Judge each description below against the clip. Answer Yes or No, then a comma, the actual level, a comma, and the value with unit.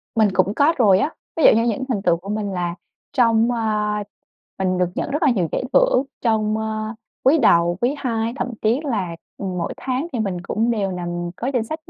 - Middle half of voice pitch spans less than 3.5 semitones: No, average, 4.6 semitones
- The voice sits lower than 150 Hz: No, high, 215 Hz